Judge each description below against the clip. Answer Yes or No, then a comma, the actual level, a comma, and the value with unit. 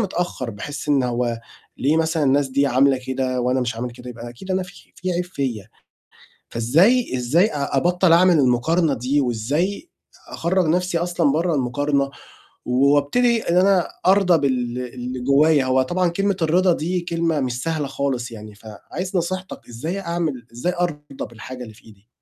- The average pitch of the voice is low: No, medium, 145 Hz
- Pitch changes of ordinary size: No, wide, 5.9 semitones